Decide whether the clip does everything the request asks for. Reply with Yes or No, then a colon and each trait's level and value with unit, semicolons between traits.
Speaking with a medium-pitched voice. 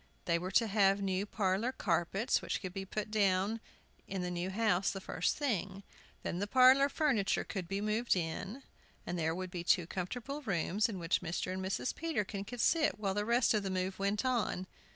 No: high, 195 Hz